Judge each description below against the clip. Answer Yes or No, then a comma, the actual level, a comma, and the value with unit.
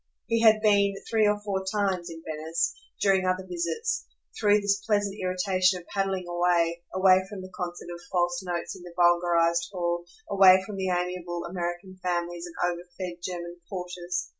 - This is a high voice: No, medium, 180 Hz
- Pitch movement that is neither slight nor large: No, narrow, 1.9 semitones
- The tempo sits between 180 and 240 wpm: No, average, 165 wpm